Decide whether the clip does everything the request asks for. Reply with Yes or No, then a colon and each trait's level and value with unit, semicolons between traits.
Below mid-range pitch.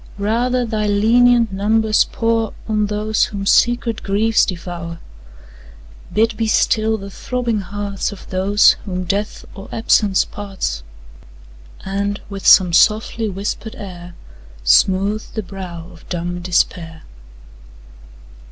No: high, 205 Hz